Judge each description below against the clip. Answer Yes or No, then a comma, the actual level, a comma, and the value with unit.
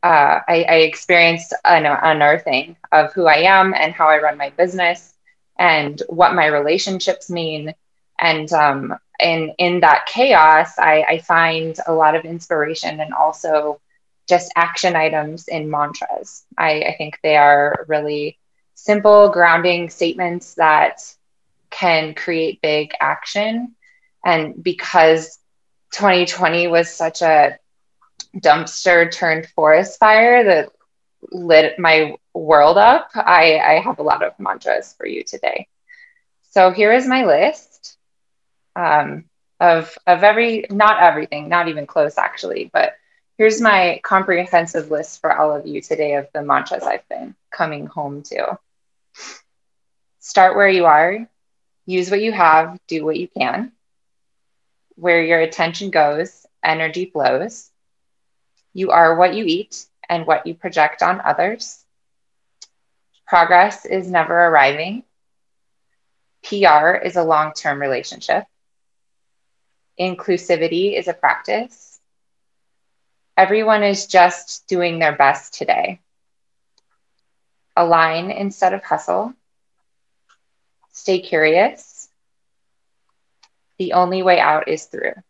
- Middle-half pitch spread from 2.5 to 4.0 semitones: Yes, average, 3.6 semitones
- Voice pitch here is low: No, medium, 170 Hz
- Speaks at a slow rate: Yes, slow, 125 wpm